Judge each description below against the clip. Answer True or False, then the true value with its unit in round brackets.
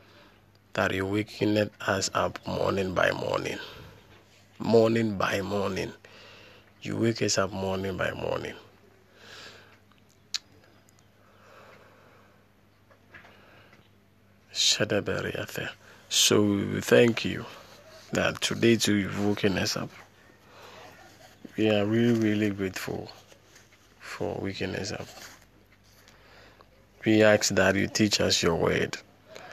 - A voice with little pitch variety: True (1.6 semitones)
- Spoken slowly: True (90 wpm)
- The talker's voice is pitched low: True (105 Hz)